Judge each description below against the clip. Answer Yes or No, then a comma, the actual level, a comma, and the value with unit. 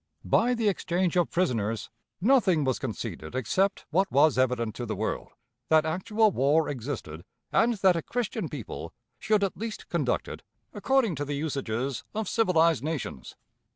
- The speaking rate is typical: Yes, average, 155 wpm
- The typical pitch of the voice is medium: Yes, medium, 160 Hz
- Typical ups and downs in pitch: No, wide, 7.5 semitones